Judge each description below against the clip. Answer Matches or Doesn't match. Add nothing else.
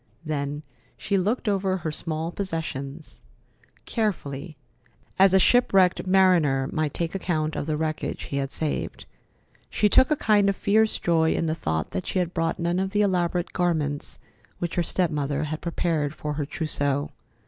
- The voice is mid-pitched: Matches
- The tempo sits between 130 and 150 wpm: Doesn't match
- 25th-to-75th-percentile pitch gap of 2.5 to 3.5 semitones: Doesn't match